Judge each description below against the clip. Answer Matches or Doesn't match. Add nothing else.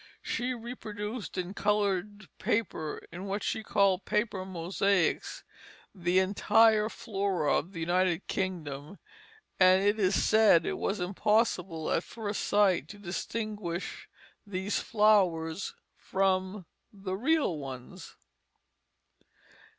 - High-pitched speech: Matches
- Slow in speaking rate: Matches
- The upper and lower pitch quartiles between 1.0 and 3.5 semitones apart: Matches